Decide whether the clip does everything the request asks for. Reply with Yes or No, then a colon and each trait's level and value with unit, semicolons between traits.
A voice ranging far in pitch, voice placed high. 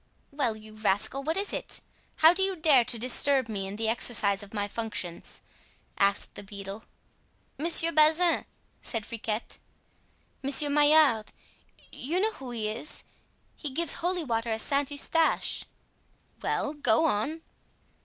Yes: wide, 6.3 semitones; very high, 260 Hz